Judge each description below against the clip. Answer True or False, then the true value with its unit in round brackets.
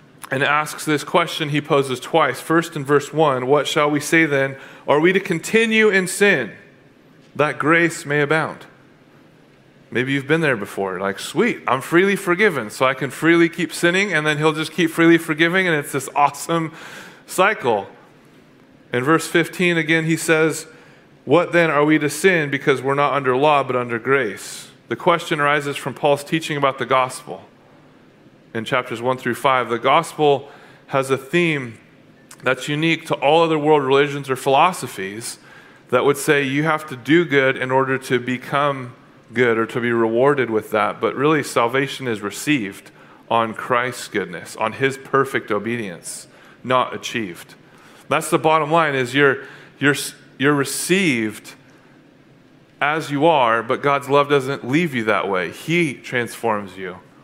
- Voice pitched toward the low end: False (145 Hz)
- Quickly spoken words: False (165 wpm)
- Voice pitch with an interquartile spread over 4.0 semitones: False (3.6 semitones)